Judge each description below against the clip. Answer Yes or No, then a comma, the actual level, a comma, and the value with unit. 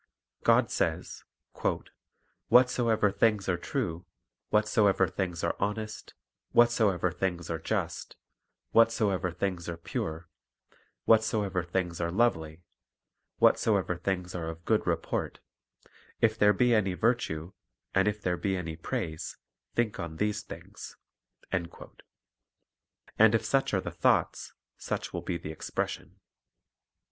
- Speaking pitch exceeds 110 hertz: No, very low, 95 Hz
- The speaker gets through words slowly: Yes, slow, 120 wpm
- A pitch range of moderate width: Yes, average, 4.1 semitones